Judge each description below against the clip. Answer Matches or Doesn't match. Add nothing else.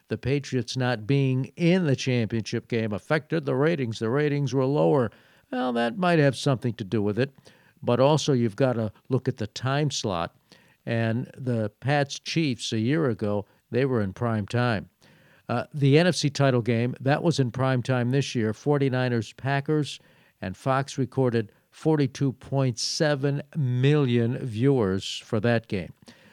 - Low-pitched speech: Matches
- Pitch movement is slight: Doesn't match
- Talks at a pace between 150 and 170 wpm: Matches